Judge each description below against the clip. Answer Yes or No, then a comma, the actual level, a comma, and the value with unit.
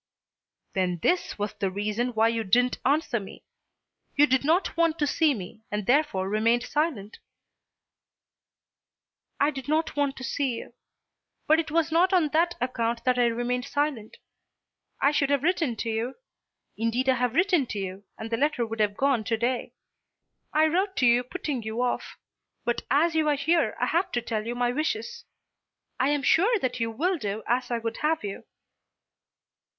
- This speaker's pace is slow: No, average, 180 wpm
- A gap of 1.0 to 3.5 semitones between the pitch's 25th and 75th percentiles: No, average, 5.2 semitones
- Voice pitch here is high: Yes, very high, 255 Hz